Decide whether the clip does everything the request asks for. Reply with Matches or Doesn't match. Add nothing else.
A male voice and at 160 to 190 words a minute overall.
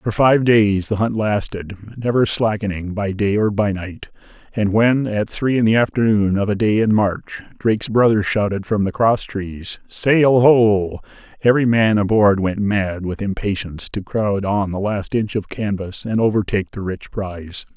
Matches